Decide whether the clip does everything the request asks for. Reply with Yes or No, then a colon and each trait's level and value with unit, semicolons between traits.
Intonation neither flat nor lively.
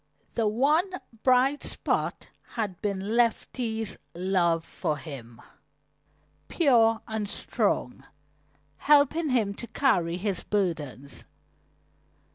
No: wide, 6.3 semitones